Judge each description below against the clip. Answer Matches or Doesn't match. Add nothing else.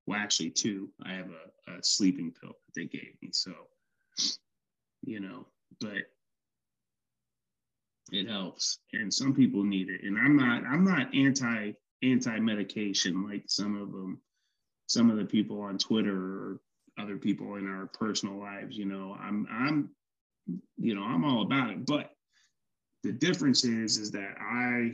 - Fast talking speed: Doesn't match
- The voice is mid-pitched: Doesn't match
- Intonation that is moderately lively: Doesn't match